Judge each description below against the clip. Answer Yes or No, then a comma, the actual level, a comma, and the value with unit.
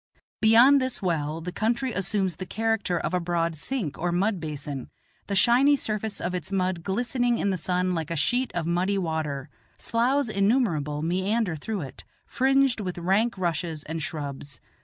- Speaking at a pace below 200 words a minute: Yes, average, 170 wpm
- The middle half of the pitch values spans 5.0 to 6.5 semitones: Yes, wide, 5.4 semitones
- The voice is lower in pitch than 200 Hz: Yes, medium, 185 Hz